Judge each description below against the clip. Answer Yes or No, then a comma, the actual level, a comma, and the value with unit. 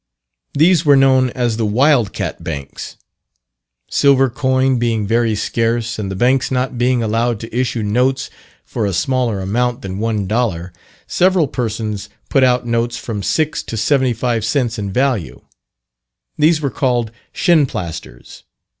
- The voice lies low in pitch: Yes, low, 120 Hz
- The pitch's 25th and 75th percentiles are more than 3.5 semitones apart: No, average, 3.2 semitones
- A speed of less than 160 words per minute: Yes, average, 145 wpm